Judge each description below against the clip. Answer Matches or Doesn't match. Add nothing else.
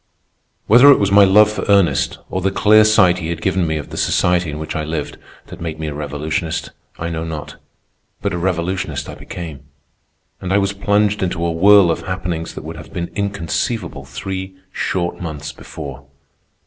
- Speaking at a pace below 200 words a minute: Matches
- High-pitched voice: Doesn't match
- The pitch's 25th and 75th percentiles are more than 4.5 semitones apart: Doesn't match